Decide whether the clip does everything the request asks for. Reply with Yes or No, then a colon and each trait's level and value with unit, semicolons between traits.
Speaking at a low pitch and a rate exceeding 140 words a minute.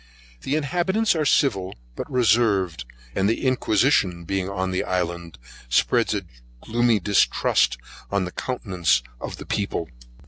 No: low, 100 Hz; slow, 135 wpm